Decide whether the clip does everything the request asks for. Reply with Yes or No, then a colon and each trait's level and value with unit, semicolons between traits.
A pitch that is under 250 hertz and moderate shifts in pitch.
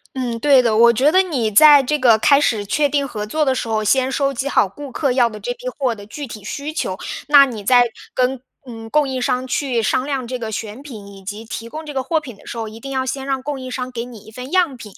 No: very high, 255 Hz; average, 3.8 semitones